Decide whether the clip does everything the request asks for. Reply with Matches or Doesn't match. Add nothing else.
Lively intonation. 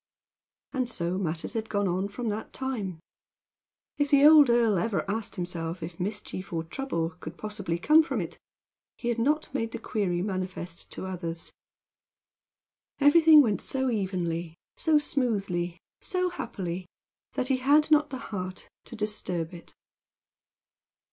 Matches